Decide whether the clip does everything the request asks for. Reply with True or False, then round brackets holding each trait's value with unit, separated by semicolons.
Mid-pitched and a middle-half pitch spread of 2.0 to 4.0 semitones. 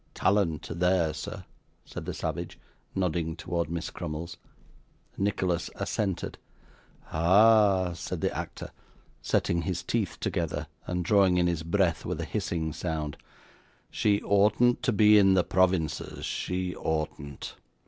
False (90 Hz; 2.9 semitones)